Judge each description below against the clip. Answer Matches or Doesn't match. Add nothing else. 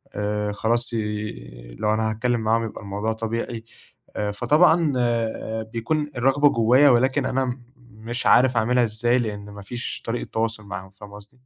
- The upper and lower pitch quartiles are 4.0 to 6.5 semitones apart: Doesn't match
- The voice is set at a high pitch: Doesn't match